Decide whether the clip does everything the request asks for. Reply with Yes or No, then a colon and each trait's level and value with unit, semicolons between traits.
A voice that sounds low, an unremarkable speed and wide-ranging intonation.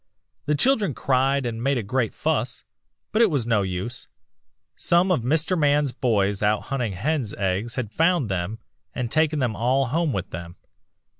Yes: low, 125 Hz; average, 170 wpm; wide, 5.9 semitones